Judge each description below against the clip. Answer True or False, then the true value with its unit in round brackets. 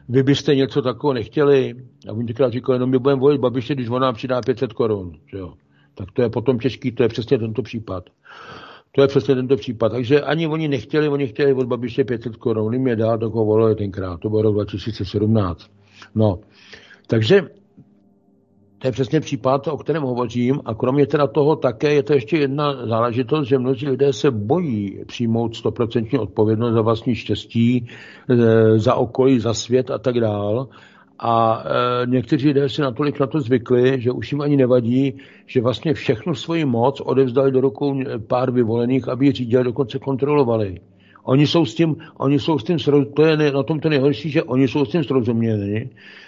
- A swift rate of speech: True (185 wpm)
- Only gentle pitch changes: False (3.5 semitones)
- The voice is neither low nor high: False (130 Hz)